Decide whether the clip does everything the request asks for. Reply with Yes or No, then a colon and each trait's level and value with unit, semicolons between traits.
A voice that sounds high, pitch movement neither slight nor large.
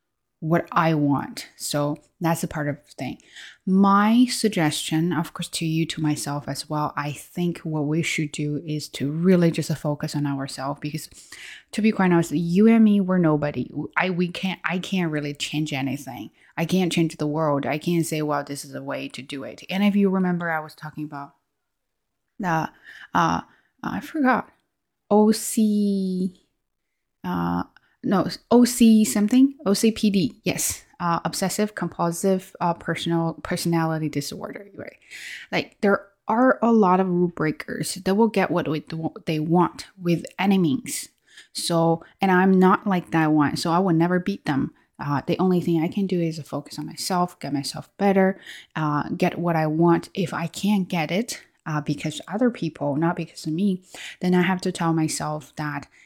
No: medium, 170 Hz; average, 3.9 semitones